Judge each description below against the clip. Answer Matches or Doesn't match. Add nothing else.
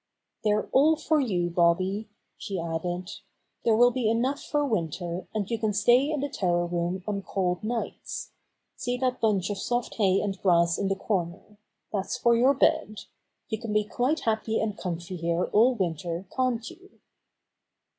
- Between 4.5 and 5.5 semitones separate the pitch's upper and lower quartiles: Matches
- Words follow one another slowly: Doesn't match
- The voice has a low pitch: Doesn't match